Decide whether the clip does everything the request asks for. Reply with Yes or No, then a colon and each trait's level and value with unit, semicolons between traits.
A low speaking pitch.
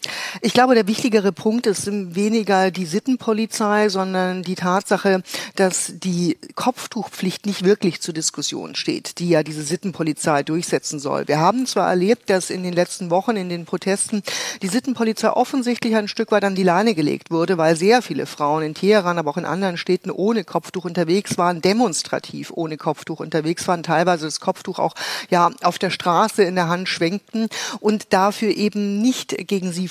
No: high, 190 Hz